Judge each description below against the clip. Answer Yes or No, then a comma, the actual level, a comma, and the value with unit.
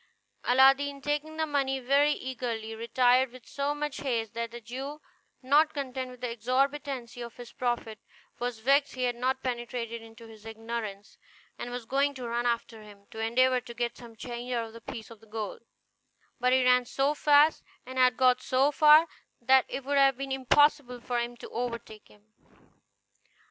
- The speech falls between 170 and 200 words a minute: Yes, average, 180 wpm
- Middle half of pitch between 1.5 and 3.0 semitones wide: Yes, average, 2.7 semitones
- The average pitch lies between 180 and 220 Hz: No, very high, 250 Hz